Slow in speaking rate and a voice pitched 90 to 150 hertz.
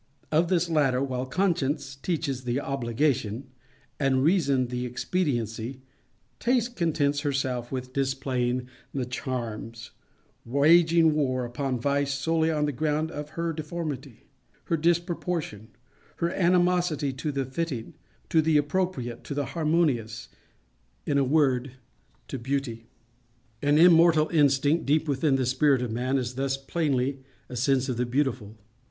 Yes: slow, 125 wpm; medium, 140 Hz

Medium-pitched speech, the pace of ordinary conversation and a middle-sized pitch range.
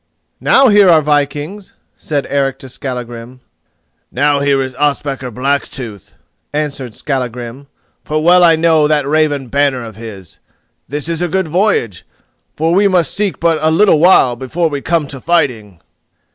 Yes: medium, 145 Hz; average, 155 wpm; average, 4.1 semitones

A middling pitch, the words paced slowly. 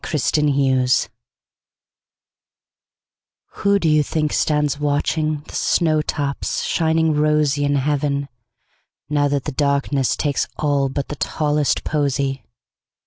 Yes: medium, 145 Hz; slow, 100 wpm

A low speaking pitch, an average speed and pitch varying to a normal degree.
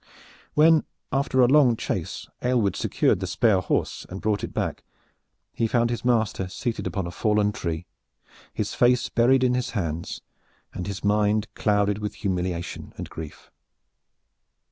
Yes: low, 105 Hz; average, 150 wpm; average, 4.2 semitones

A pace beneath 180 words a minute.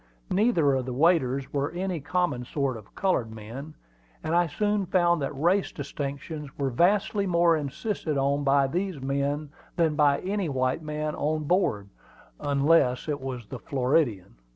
Yes: average, 155 wpm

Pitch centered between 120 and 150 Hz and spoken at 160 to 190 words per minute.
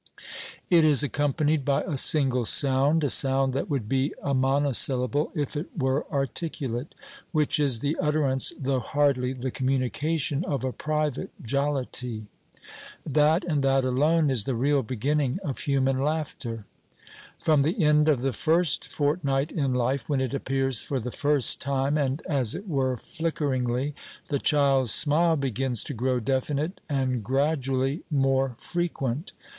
No: medium, 140 Hz; average, 150 wpm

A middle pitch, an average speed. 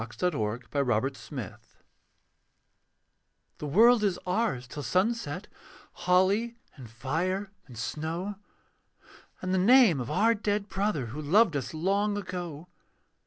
No: medium, 180 Hz; slow, 125 wpm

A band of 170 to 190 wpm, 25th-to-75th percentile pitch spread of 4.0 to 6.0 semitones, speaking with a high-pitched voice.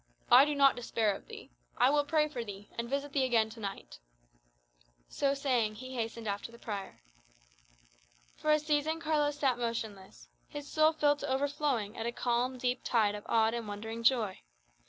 Yes: average, 180 wpm; average, 4.5 semitones; high, 245 Hz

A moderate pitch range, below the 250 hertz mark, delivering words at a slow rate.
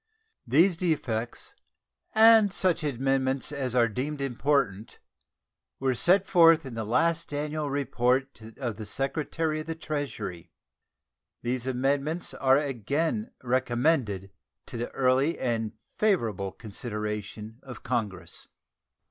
Yes: average, 4.8 semitones; low, 135 Hz; slow, 115 wpm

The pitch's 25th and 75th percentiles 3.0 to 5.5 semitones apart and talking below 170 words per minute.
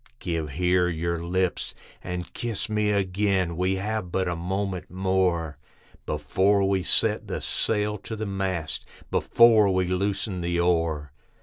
No: narrow, 2.5 semitones; average, 140 wpm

